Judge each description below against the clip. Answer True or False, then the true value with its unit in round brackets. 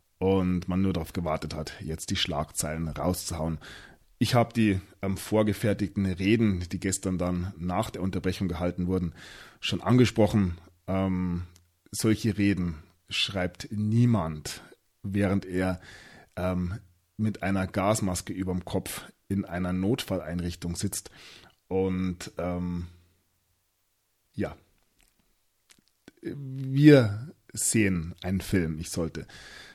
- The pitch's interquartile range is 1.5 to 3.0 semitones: True (2.4 semitones)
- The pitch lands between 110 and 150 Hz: False (95 Hz)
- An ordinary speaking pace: False (105 wpm)